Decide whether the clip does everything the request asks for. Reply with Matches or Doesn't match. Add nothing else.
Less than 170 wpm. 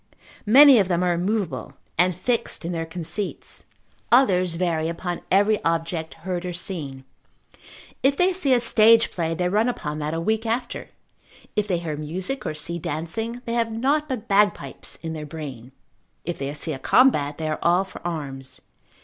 Doesn't match